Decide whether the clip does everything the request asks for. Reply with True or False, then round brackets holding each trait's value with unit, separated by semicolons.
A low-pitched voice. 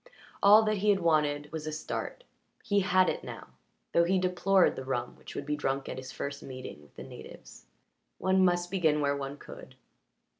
False (155 Hz)